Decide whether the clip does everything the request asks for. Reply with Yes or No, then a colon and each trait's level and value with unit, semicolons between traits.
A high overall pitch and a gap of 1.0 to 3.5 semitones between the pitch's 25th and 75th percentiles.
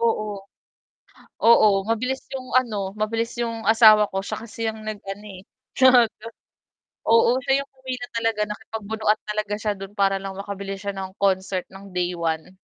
Yes: high, 210 Hz; average, 2.8 semitones